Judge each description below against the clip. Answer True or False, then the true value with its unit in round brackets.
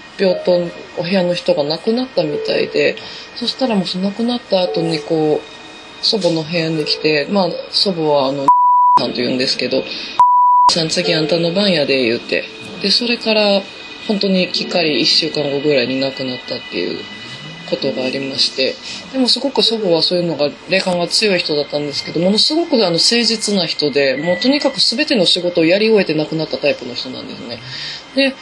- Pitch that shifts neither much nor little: False (6.6 semitones)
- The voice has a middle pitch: True (180 Hz)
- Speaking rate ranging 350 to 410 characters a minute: True (385 characters per minute)